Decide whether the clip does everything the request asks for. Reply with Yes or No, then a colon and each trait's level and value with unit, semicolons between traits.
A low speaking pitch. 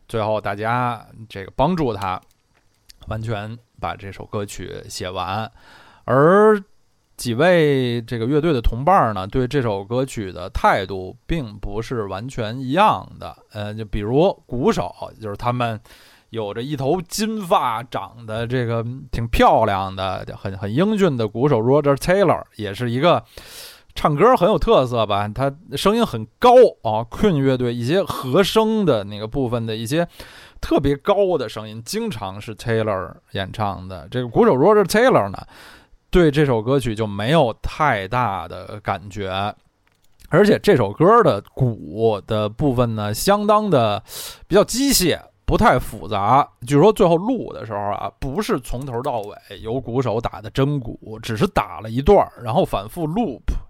Yes: low, 115 Hz